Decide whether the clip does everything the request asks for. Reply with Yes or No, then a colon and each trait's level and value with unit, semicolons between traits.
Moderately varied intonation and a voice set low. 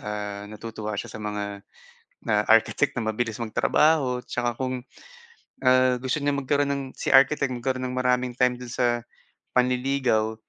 Yes: average, 3.0 semitones; low, 125 Hz